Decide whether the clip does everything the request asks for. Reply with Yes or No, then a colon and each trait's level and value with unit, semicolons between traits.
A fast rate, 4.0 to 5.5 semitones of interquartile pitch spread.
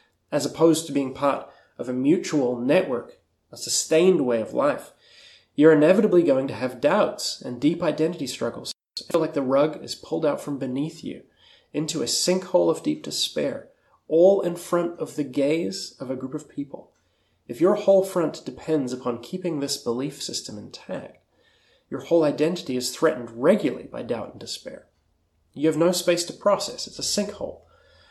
No: average, 175 wpm; average, 4.4 semitones